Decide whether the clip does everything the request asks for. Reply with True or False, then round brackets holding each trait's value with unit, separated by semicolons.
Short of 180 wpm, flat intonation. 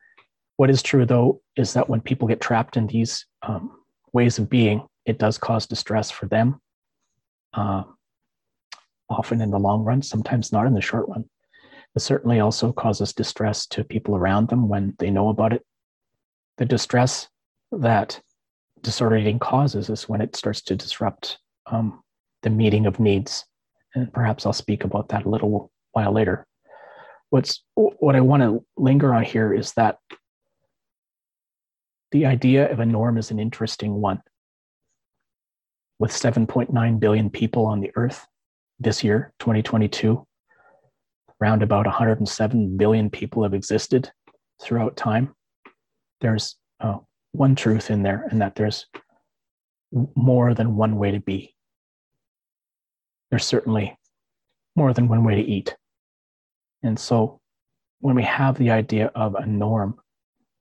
True (145 wpm; 2.3 semitones)